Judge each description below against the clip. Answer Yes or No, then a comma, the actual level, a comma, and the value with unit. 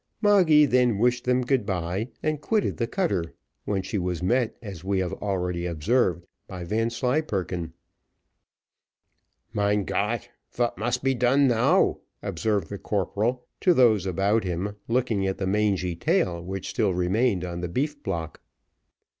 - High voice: No, low, 105 Hz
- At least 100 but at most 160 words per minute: Yes, average, 145 wpm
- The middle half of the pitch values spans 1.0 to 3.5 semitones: No, average, 5.3 semitones